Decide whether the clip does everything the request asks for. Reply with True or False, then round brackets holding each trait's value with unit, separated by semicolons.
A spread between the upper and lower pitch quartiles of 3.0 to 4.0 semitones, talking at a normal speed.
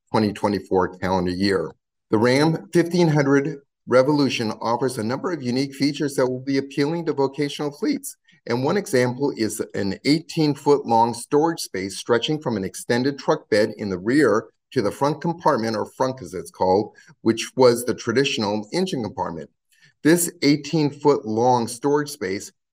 False (4.9 semitones; 160 wpm)